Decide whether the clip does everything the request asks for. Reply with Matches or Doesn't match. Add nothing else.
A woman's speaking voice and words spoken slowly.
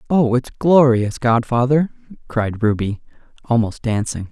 Doesn't match